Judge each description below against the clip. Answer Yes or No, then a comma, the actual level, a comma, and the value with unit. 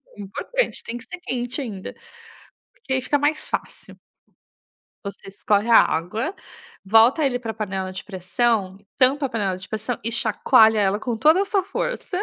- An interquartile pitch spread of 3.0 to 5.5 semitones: Yes, average, 5.2 semitones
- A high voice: Yes, high, 230 Hz